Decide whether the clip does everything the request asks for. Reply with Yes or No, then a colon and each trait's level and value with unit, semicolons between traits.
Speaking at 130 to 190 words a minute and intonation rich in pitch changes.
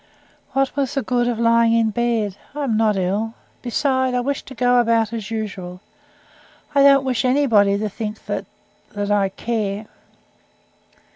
No: average, 160 wpm; average, 3.2 semitones